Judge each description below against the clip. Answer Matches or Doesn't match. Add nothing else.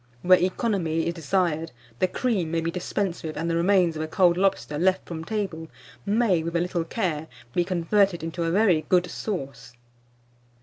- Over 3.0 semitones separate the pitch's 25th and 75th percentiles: Doesn't match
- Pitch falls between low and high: Matches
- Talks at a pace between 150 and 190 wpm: Matches